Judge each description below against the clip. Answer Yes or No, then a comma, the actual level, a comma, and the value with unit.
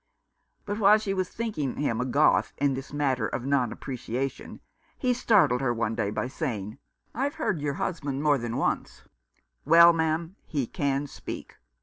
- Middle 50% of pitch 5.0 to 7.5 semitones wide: Yes, wide, 5.4 semitones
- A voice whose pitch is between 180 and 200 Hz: No, medium, 140 Hz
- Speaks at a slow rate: No, average, 175 wpm